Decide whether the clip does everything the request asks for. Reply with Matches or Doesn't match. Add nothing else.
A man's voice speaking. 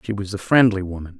Matches